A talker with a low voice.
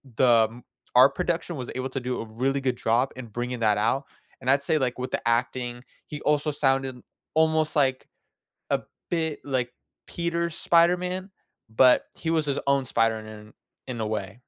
Yes: low, 130 Hz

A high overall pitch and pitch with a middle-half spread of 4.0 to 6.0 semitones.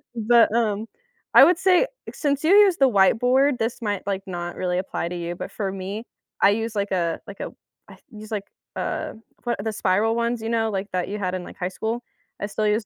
No: high, 215 Hz; average, 3.6 semitones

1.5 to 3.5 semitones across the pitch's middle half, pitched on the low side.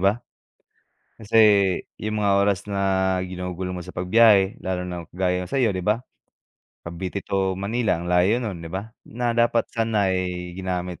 Yes: average, 3.0 semitones; very low, 95 Hz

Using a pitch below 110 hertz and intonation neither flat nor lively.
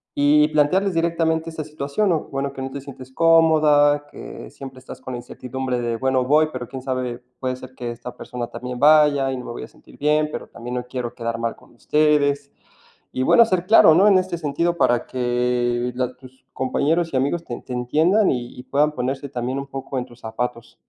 No: low, 135 Hz; average, 3.6 semitones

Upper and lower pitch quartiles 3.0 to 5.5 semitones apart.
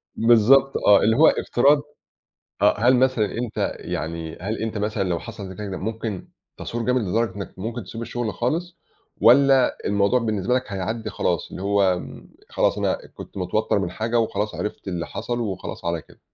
Yes: average, 3.6 semitones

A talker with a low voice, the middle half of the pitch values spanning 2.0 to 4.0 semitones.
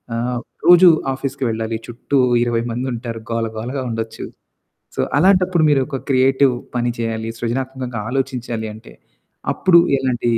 Yes: low, 125 Hz; average, 2.8 semitones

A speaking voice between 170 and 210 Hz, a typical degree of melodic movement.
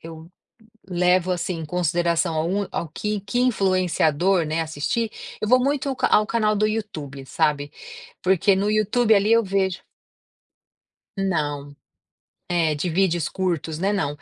Yes: medium, 185 Hz; average, 4.5 semitones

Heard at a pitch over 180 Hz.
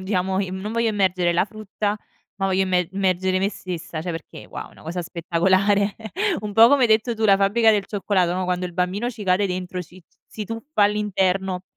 Yes: high, 190 Hz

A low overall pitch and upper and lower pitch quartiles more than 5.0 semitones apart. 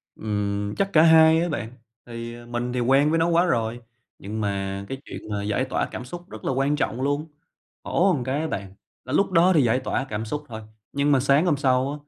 Yes: low, 130 Hz; wide, 5.4 semitones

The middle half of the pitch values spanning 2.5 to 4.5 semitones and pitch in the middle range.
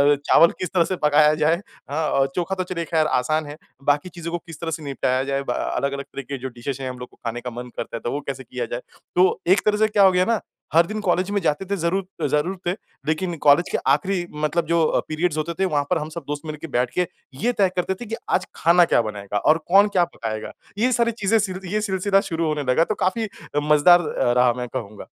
No: average, 5.0 semitones; medium, 165 Hz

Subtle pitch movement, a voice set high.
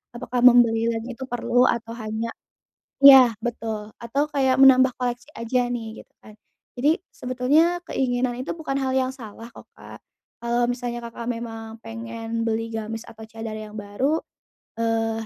Yes: narrow, 2.2 semitones; high, 235 Hz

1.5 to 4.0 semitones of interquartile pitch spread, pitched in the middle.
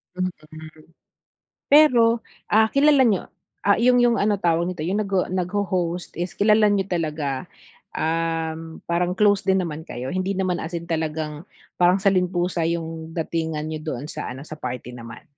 Yes: average, 3.6 semitones; medium, 175 Hz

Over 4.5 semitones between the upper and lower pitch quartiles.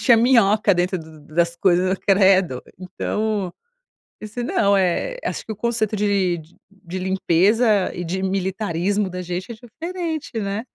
No: average, 3.0 semitones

